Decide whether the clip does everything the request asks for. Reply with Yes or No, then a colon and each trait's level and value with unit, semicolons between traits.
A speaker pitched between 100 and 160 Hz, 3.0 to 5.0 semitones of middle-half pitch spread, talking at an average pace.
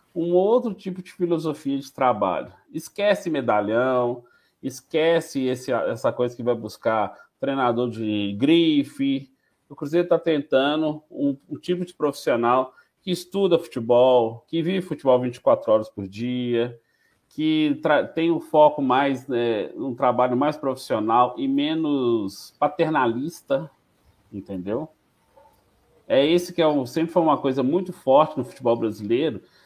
No: medium, 140 Hz; wide, 5.5 semitones; average, 135 wpm